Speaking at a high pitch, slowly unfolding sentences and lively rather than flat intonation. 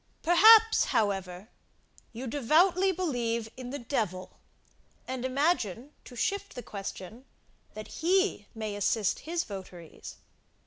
Yes: high, 245 Hz; slow, 115 wpm; wide, 8.5 semitones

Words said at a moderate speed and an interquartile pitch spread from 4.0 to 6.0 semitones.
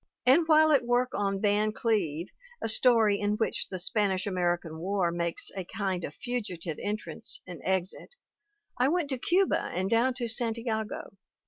Yes: average, 160 wpm; average, 4.6 semitones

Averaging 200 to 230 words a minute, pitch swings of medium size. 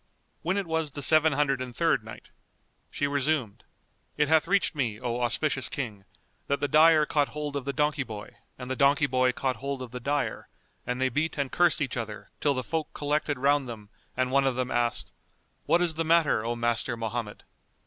Yes: fast, 205 wpm; average, 3.5 semitones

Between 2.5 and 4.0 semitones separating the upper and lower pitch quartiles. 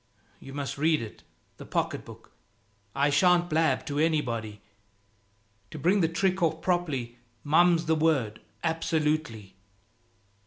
Yes: average, 3.5 semitones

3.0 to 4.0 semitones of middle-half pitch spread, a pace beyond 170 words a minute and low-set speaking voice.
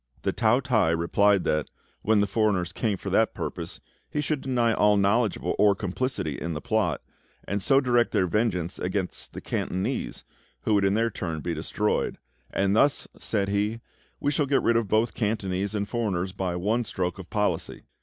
Yes: average, 3.7 semitones; average, 185 wpm; low, 105 Hz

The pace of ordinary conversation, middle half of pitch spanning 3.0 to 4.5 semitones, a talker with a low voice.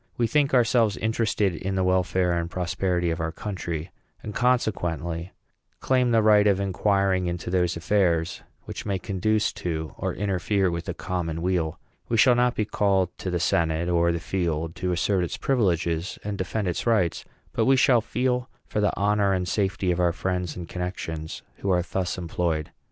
Yes: average, 180 wpm; average, 3.4 semitones; very low, 95 Hz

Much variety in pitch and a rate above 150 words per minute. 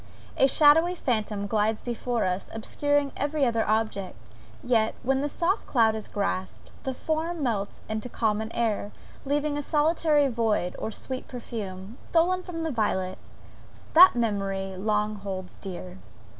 No: wide, 5.8 semitones; average, 145 wpm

